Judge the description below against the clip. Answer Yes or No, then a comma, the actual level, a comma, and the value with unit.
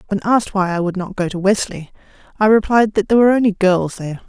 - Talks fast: Yes, fast, 240 wpm